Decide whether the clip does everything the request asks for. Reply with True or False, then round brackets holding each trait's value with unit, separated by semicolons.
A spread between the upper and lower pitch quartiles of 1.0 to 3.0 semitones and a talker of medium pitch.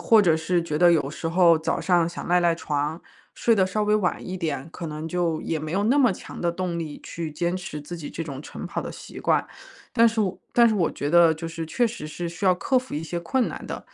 True (2.7 semitones; 170 Hz)